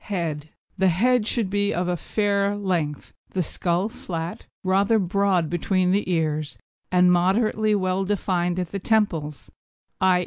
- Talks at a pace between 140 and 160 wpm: Yes, average, 145 wpm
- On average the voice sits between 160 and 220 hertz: Yes, medium, 185 Hz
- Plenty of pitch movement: No, average, 2.7 semitones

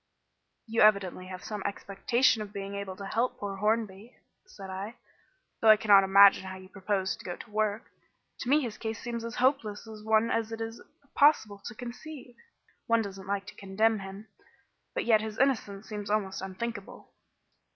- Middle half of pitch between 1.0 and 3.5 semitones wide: Yes, narrow, 2.5 semitones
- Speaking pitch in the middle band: No, high, 210 Hz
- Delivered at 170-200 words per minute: Yes, average, 180 wpm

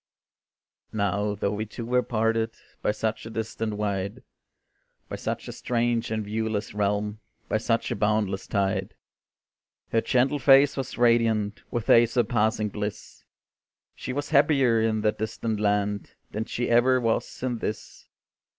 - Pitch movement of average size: No, narrow, 2.2 semitones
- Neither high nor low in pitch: No, low, 110 Hz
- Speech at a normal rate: Yes, average, 145 wpm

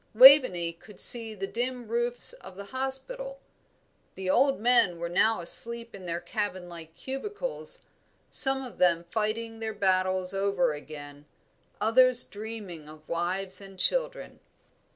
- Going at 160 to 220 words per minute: No, average, 140 wpm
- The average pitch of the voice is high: Yes, high, 210 Hz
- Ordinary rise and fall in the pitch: No, wide, 5.8 semitones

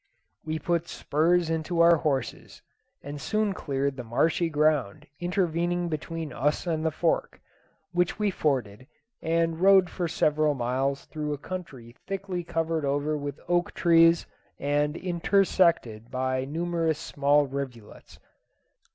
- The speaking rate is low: Yes, slow, 130 wpm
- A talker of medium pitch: Yes, medium, 160 Hz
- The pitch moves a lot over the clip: No, average, 3.5 semitones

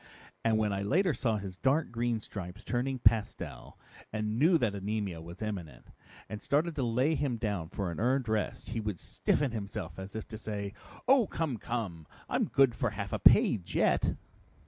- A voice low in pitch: Yes, low, 110 Hz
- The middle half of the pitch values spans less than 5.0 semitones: Yes, average, 4.0 semitones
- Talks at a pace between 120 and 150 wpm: No, average, 185 wpm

